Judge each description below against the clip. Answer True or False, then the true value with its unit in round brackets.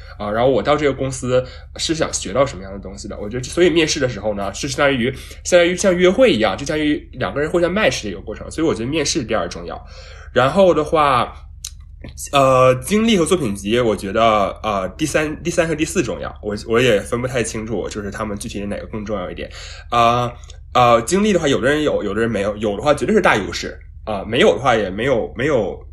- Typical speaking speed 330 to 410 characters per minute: True (365 characters per minute)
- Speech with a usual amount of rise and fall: False (7.2 semitones)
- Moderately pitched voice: False (120 Hz)